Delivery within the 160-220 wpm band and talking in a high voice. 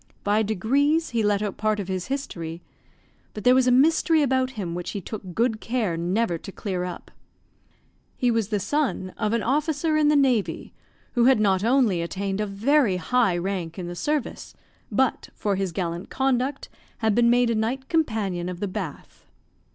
Yes: average, 185 wpm; high, 215 Hz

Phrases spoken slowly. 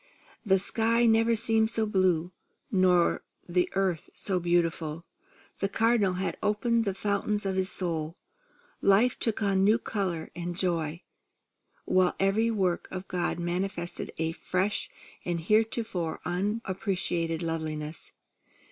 Yes: slow, 130 wpm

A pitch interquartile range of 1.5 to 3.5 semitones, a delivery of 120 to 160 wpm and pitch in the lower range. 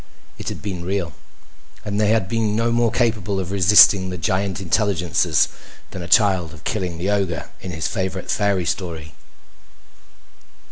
Yes: average, 2.8 semitones; average, 155 wpm; very low, 95 Hz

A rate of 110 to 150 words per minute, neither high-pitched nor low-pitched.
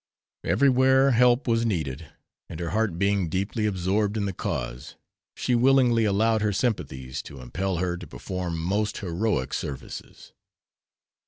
No: average, 140 wpm; low, 100 Hz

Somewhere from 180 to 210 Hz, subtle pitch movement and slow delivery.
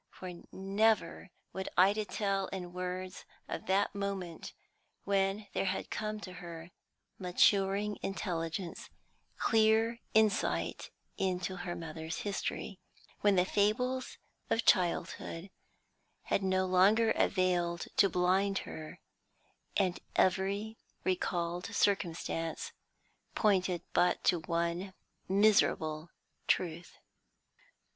Yes: high, 190 Hz; narrow, 2.3 semitones; slow, 100 wpm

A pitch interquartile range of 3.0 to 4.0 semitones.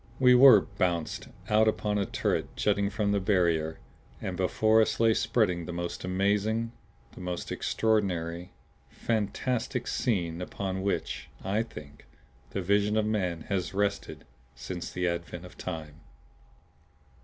Yes: average, 3.6 semitones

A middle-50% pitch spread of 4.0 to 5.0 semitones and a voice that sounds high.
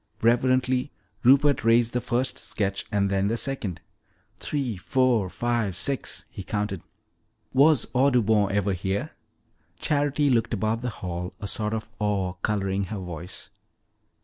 No: average, 4.5 semitones; low, 110 Hz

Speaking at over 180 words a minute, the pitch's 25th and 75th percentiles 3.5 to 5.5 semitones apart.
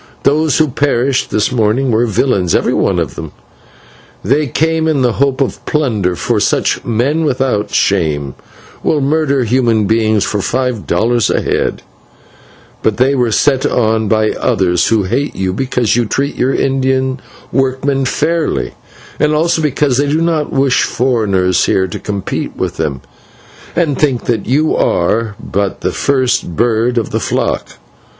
No: average, 155 wpm; average, 4.4 semitones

